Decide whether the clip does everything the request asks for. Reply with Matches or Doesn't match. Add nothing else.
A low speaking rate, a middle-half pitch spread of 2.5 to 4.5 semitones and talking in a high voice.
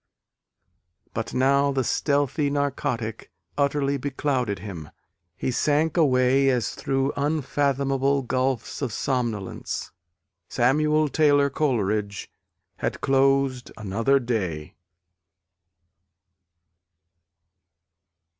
Doesn't match